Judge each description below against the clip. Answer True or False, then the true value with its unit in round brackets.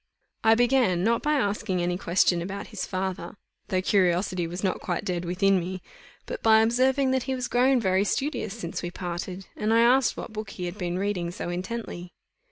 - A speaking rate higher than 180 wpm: True (195 wpm)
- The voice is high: True (195 Hz)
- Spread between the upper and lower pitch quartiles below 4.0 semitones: False (4.6 semitones)